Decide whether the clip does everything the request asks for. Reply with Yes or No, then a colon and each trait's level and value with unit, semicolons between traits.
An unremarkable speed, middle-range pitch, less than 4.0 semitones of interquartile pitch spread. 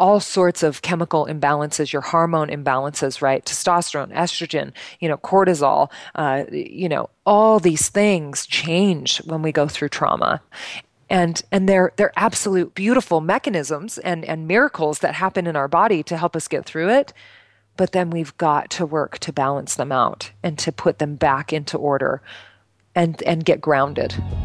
Yes: average, 165 wpm; medium, 165 Hz; average, 3.5 semitones